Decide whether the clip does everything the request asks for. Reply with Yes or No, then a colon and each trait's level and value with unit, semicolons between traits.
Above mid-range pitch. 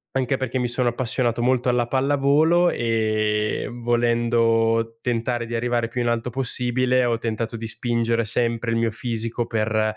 No: low, 120 Hz